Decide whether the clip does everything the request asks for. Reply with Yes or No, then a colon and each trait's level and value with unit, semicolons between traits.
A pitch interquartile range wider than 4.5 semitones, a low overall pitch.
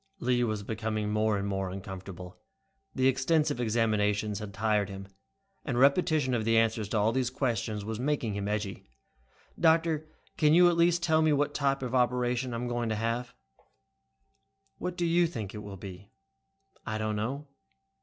Yes: average, 4.9 semitones; low, 115 Hz